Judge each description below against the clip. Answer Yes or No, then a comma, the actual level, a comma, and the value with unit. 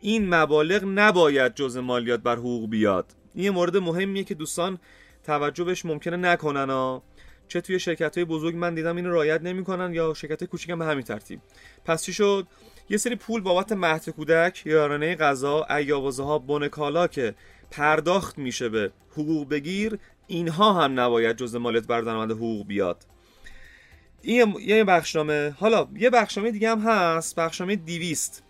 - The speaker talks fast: Yes, fast, 160 wpm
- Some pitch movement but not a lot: Yes, average, 4.7 semitones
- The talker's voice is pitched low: No, medium, 165 Hz